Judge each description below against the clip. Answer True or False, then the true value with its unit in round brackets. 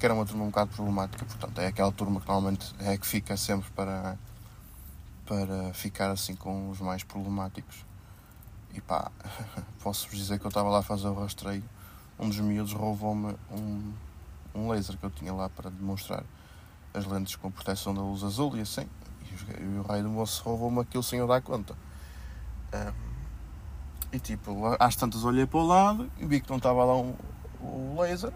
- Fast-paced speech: True (195 wpm)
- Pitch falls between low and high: False (100 Hz)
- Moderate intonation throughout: False (2.3 semitones)